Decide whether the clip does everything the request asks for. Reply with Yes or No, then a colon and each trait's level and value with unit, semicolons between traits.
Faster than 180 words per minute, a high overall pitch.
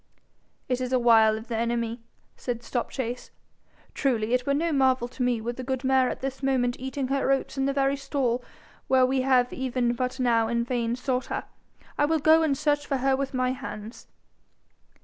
Yes: average, 200 wpm; very high, 255 Hz